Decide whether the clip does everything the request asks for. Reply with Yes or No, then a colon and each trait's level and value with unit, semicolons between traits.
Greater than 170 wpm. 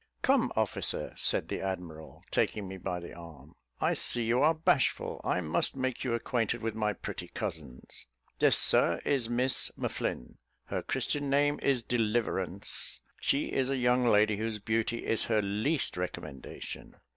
No: average, 155 wpm